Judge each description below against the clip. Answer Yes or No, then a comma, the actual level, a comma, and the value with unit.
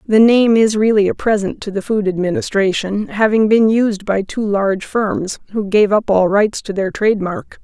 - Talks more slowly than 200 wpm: No, fast, 205 wpm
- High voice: Yes, high, 205 Hz